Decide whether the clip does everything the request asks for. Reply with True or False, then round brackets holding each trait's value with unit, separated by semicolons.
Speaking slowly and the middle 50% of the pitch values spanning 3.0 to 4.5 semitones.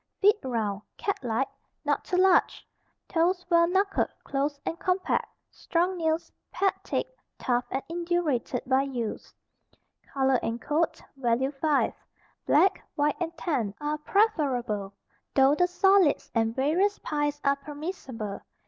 False (130 wpm; 5.2 semitones)